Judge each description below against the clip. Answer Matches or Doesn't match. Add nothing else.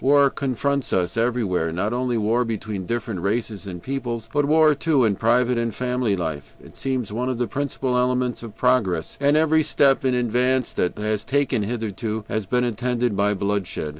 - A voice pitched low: Matches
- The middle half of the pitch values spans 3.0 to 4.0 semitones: Matches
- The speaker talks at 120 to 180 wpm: Doesn't match